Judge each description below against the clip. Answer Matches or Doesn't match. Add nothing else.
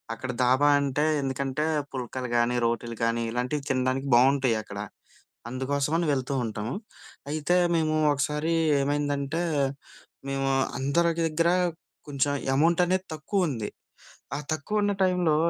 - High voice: Doesn't match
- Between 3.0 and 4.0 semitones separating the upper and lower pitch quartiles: Matches